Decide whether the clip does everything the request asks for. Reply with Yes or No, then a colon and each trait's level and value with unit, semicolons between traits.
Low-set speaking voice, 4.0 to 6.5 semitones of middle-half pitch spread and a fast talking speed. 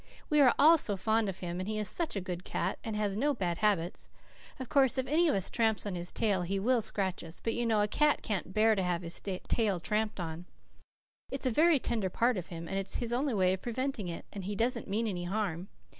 No: high, 210 Hz; average, 4.4 semitones; fast, 250 wpm